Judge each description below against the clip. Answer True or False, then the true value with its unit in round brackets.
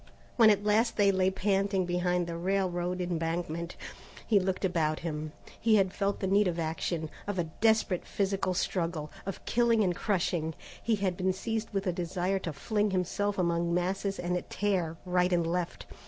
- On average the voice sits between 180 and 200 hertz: True (185 Hz)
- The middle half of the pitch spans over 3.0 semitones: False (2.6 semitones)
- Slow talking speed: False (175 wpm)